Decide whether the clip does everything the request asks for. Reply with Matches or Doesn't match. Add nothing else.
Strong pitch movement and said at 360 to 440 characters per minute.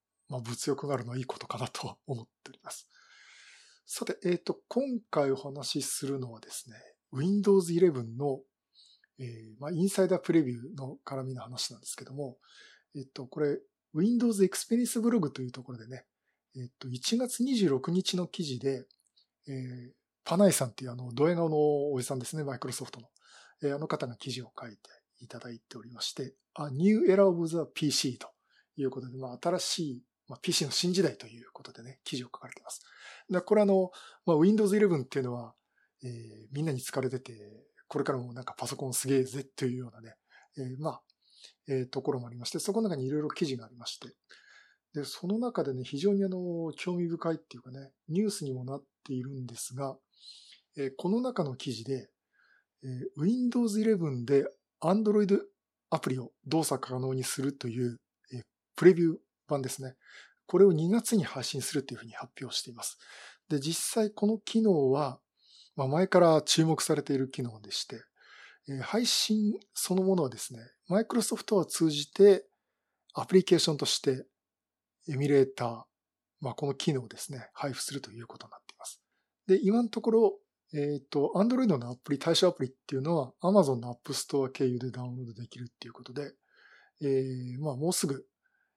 Matches